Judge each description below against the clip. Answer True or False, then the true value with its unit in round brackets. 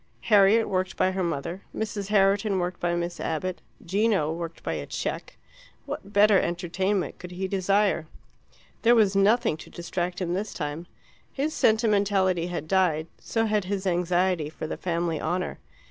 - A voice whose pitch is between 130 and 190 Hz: True (185 Hz)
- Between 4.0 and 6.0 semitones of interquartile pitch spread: False (2.8 semitones)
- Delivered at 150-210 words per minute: True (160 wpm)